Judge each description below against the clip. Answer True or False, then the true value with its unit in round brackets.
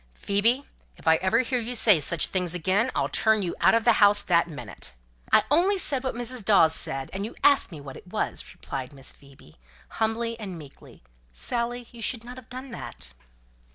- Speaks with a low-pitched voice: False (210 Hz)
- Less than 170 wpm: False (200 wpm)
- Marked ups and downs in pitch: True (6.6 semitones)